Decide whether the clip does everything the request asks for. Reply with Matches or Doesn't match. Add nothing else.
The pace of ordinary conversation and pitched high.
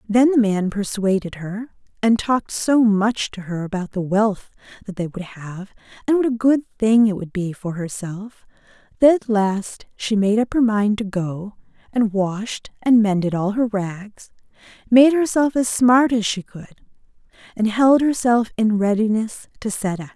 Matches